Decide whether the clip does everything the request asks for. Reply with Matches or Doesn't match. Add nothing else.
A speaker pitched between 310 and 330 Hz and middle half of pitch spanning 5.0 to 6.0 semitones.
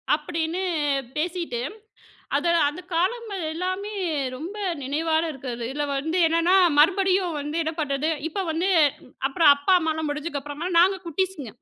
Doesn't match